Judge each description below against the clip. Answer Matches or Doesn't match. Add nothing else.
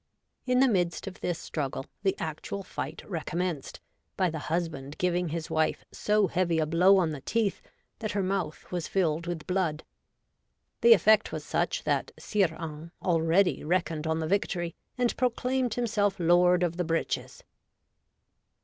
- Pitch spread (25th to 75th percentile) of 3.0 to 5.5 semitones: Matches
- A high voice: Doesn't match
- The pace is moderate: Matches